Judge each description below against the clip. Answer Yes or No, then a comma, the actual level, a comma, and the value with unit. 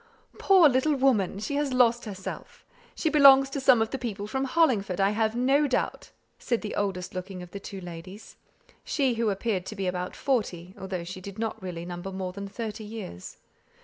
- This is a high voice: Yes, high, 210 Hz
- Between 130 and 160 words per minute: No, average, 195 wpm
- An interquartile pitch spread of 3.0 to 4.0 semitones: No, wide, 5.5 semitones